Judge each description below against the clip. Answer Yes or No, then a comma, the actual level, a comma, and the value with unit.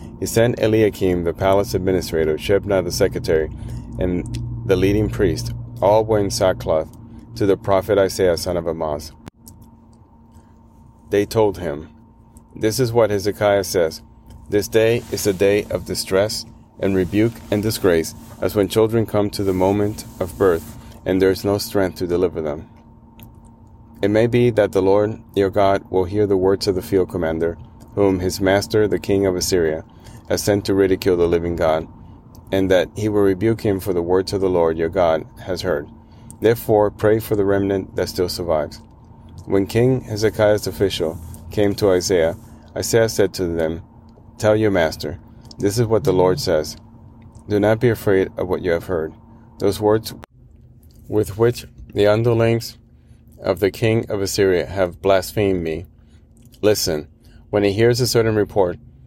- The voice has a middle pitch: No, low, 100 Hz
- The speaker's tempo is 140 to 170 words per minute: Yes, average, 165 wpm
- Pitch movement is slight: No, average, 3.3 semitones